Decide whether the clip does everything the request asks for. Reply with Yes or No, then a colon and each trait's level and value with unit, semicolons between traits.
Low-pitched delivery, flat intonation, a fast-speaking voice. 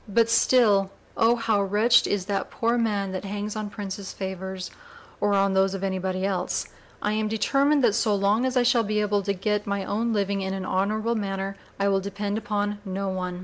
No: high, 205 Hz; narrow, 1.9 semitones; fast, 210 wpm